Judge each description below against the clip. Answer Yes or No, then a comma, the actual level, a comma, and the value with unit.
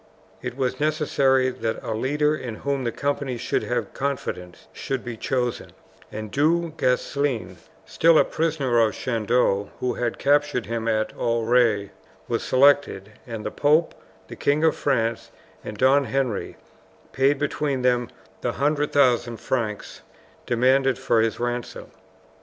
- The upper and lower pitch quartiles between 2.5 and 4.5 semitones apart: Yes, average, 3.5 semitones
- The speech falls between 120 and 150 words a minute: Yes, average, 140 wpm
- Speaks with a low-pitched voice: Yes, low, 125 Hz